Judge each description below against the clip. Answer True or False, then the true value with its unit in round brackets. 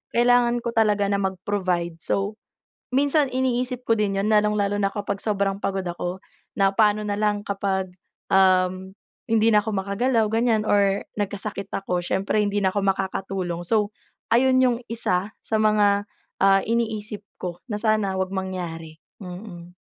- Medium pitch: False (200 Hz)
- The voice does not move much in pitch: True (2.3 semitones)